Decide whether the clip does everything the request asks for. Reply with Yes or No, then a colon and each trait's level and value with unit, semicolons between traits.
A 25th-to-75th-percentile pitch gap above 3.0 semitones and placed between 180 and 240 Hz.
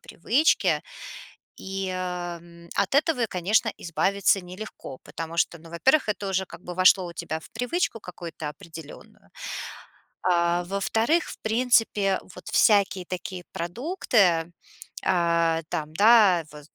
Yes: average, 4.1 semitones; medium, 185 Hz